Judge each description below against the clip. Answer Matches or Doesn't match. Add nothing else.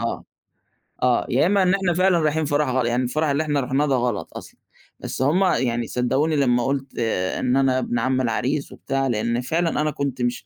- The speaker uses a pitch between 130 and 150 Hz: Matches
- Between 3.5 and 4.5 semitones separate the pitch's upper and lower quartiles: Matches